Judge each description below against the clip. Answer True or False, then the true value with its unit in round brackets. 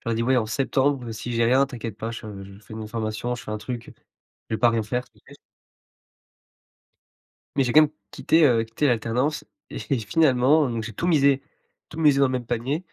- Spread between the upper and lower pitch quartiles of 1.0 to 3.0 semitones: False (3.4 semitones)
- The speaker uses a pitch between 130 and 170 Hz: False (120 Hz)